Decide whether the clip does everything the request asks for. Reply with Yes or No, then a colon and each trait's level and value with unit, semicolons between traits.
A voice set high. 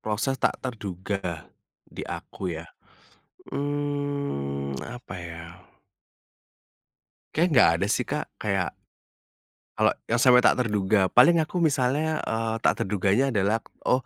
No: low, 110 Hz